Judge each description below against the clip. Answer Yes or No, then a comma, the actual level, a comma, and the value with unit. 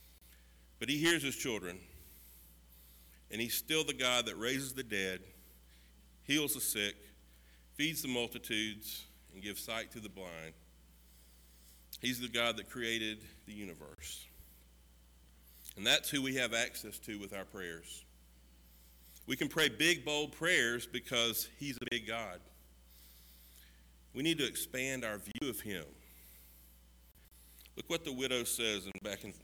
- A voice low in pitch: Yes, very low, 90 Hz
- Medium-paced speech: Yes, average, 145 wpm